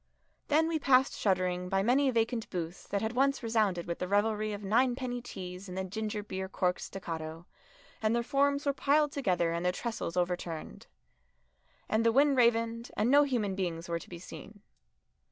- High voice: Yes, high, 215 Hz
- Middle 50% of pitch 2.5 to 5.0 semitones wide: No, wide, 5.4 semitones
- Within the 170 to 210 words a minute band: Yes, average, 175 wpm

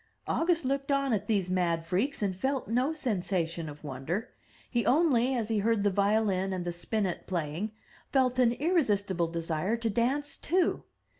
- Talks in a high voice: Yes, high, 215 Hz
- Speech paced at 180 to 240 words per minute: No, average, 165 wpm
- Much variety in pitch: Yes, wide, 6.3 semitones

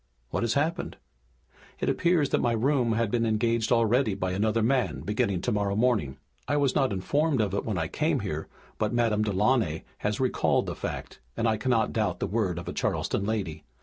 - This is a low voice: Yes, low, 110 Hz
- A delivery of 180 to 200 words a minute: Yes, average, 195 wpm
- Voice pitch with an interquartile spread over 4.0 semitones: No, average, 3.4 semitones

